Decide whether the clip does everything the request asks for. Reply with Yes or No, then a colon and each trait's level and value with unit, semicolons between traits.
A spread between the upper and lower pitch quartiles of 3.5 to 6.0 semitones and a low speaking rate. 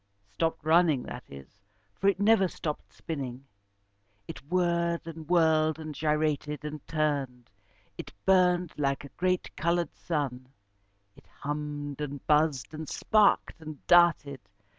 No: average, 3.1 semitones; slow, 130 wpm